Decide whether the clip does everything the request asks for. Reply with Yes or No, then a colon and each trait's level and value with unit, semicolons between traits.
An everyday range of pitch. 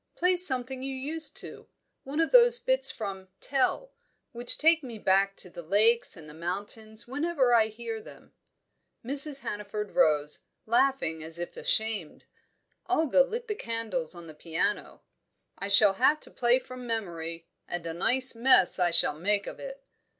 No: wide, 6.5 semitones